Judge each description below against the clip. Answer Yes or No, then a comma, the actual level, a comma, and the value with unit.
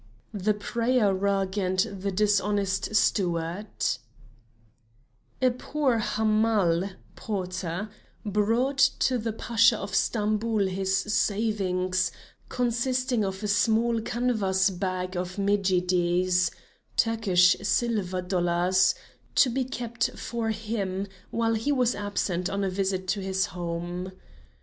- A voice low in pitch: No, high, 200 Hz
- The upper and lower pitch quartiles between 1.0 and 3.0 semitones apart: No, average, 3.4 semitones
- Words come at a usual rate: No, slow, 110 wpm